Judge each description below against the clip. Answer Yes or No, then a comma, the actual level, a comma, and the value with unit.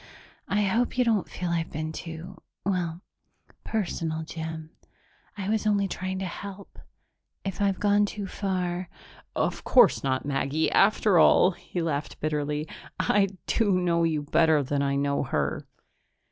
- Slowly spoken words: No, average, 150 wpm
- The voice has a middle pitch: Yes, medium, 175 Hz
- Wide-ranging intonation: No, average, 4.0 semitones